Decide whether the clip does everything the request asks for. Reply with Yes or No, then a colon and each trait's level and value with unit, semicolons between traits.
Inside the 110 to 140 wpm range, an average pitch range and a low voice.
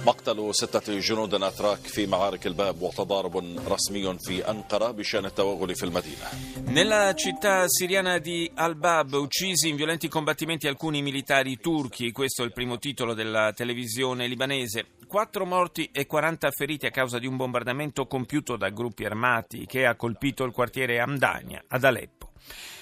Yes: average, 120 wpm; average, 5.0 semitones; low, 130 Hz